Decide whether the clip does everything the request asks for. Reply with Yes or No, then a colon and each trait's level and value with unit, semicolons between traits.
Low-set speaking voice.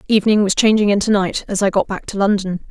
No: high, 200 Hz